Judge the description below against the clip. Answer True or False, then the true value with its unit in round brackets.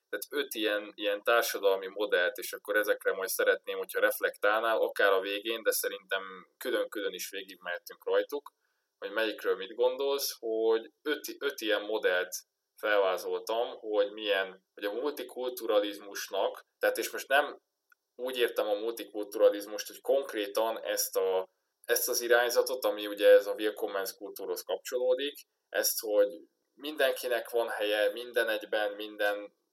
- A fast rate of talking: False (135 wpm)